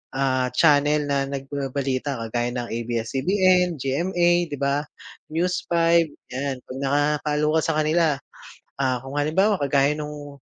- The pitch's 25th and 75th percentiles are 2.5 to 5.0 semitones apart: Yes, average, 3.0 semitones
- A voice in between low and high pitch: Yes, medium, 145 Hz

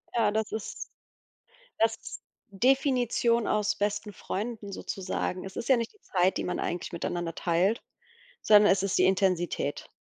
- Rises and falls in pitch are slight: No, average, 3.3 semitones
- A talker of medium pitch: No, high, 205 Hz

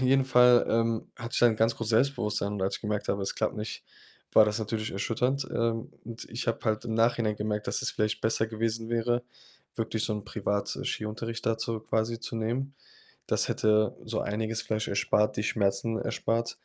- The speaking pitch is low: Yes, low, 110 Hz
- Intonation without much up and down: Yes, narrow, 1.5 semitones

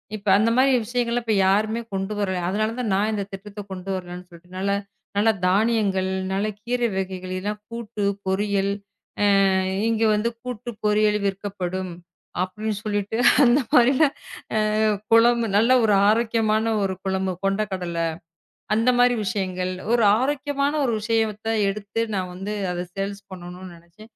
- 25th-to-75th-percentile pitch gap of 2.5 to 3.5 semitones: Yes, average, 3.1 semitones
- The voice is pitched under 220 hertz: Yes, high, 205 Hz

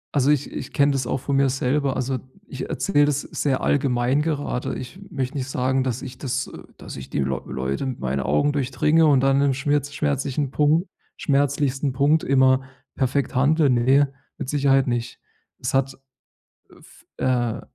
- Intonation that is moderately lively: No, narrow, 2.0 semitones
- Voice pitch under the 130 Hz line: No, low, 135 Hz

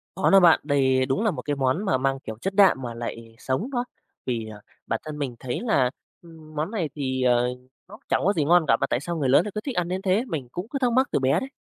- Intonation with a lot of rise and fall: Yes, wide, 6.8 semitones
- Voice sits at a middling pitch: Yes, medium, 150 Hz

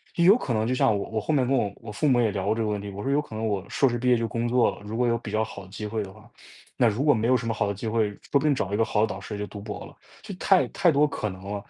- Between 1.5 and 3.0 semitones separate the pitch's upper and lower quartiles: No, average, 3.6 semitones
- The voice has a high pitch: No, low, 110 Hz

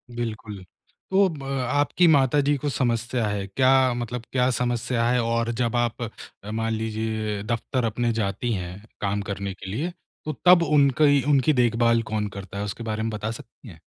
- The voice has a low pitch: Yes, low, 115 Hz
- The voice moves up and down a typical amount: Yes, average, 3.3 semitones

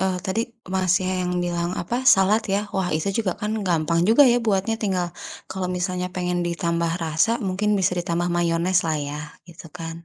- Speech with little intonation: Yes, narrow, 2.2 semitones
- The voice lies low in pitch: No, medium, 180 Hz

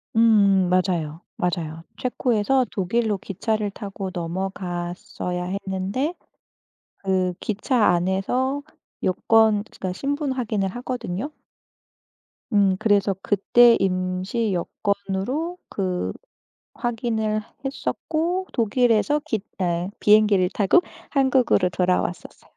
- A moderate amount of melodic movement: Yes, average, 4.5 semitones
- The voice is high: Yes, high, 200 Hz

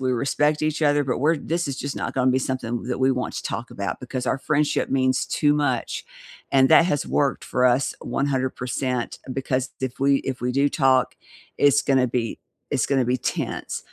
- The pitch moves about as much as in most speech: No, narrow, 2.0 semitones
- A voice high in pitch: No, low, 130 Hz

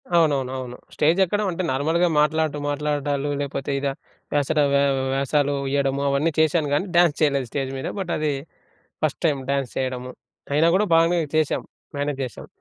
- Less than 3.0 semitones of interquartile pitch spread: Yes, narrow, 2.4 semitones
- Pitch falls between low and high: Yes, medium, 145 Hz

